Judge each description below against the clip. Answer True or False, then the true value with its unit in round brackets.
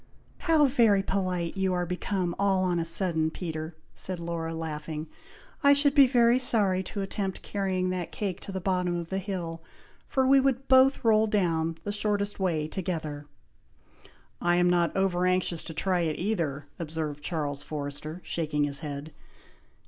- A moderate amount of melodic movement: True (3.7 semitones)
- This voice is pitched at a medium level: True (180 Hz)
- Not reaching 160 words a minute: False (165 wpm)